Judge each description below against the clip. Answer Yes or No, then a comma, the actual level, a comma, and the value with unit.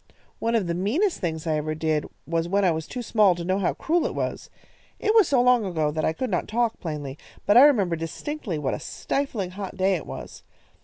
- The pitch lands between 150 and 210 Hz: Yes, medium, 185 Hz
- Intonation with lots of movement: Yes, wide, 6.8 semitones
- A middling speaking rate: No, fast, 230 wpm